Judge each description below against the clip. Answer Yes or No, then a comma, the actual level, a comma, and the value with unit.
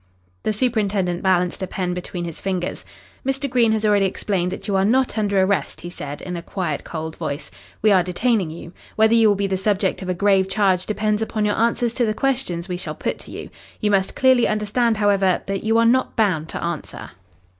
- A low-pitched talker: No, high, 200 Hz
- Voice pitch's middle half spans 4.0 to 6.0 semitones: No, average, 3.3 semitones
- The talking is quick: Yes, fast, 220 wpm